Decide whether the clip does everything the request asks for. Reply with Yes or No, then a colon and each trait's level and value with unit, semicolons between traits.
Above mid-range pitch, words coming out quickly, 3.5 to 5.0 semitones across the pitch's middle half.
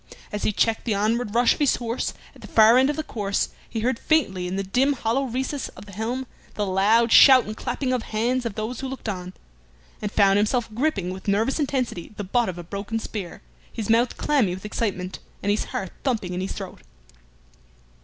Yes: high, 220 Hz; fast, 215 wpm; average, 4.0 semitones